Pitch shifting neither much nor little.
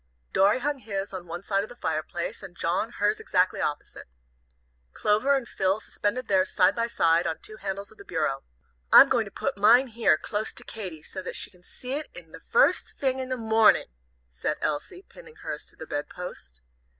Yes: average, 4.9 semitones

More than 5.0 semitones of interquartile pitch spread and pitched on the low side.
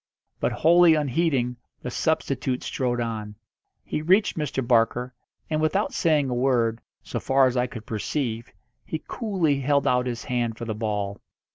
No: average, 4.5 semitones; low, 125 Hz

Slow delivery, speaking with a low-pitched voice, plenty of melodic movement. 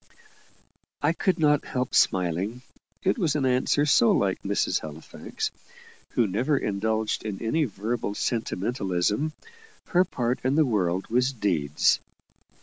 Yes: slow, 130 wpm; low, 115 Hz; wide, 6.1 semitones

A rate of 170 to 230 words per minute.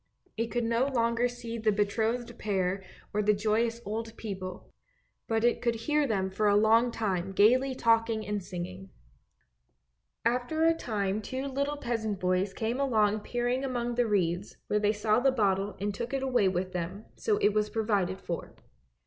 Yes: average, 175 wpm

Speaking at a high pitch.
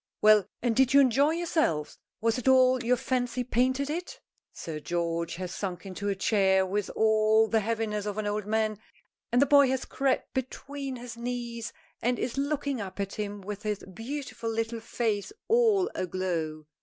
Yes: high, 225 Hz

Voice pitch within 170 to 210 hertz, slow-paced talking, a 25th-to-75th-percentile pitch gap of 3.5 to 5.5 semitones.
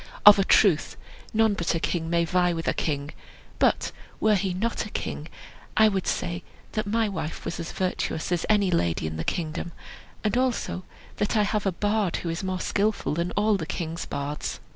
No: medium, 185 Hz; average, 200 wpm; average, 3.9 semitones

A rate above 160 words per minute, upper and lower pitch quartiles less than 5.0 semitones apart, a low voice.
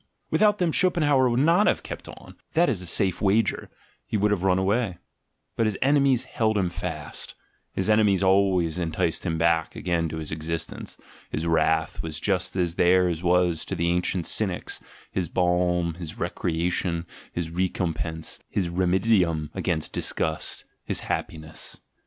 No: average, 155 wpm; average, 3.8 semitones; very low, 90 Hz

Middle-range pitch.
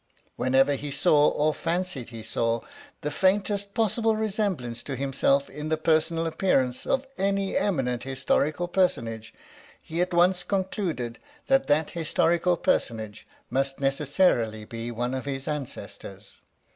Yes: medium, 150 Hz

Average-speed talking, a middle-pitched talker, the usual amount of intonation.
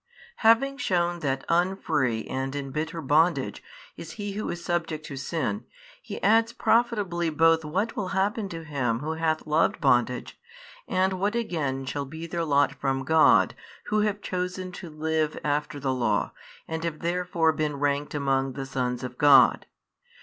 Yes: average, 165 wpm; medium, 160 Hz; average, 4.4 semitones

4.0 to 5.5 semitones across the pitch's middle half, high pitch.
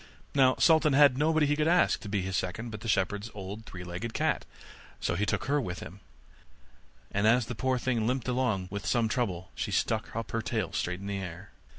No: average, 4.9 semitones; low, 110 Hz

